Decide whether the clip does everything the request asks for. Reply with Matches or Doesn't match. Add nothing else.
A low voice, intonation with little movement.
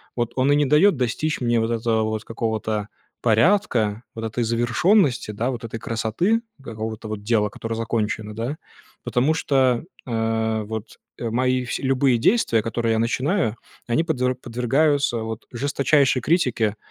Doesn't match